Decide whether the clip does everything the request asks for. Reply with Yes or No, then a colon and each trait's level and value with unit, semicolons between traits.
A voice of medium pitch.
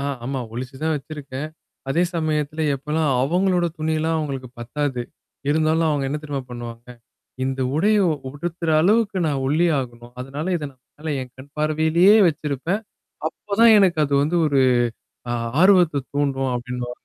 Yes: medium, 150 Hz